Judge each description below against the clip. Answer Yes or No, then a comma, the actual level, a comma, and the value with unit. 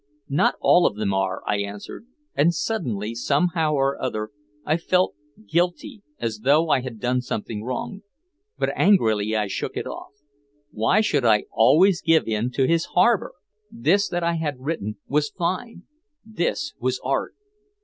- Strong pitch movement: Yes, wide, 7.7 semitones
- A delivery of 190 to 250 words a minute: No, average, 160 wpm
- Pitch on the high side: No, medium, 145 Hz